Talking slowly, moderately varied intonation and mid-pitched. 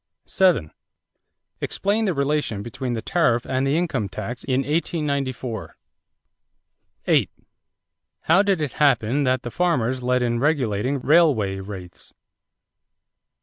No: slow, 115 wpm; average, 4.8 semitones; low, 130 Hz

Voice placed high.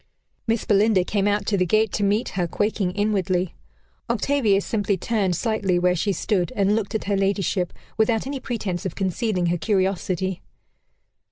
Yes: high, 200 Hz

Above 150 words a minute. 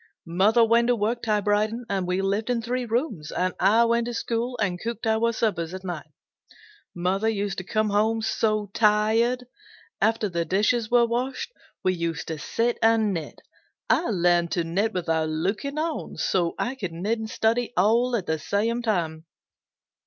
Yes: average, 175 wpm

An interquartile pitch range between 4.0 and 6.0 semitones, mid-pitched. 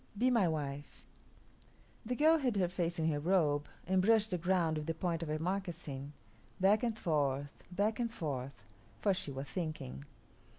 Yes: average, 5.2 semitones; medium, 170 Hz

